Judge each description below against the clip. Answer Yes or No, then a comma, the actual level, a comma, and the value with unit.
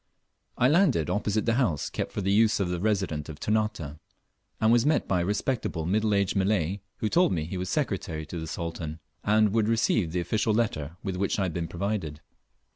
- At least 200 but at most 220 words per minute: Yes, fast, 205 wpm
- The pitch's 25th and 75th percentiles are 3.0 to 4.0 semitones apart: No, average, 4.5 semitones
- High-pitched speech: No, low, 100 Hz